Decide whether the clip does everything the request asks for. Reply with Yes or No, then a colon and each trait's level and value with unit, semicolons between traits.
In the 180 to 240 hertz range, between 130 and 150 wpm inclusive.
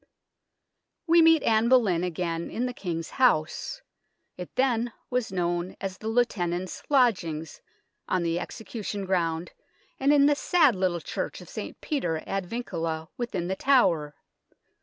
Yes: high, 190 Hz; average, 145 wpm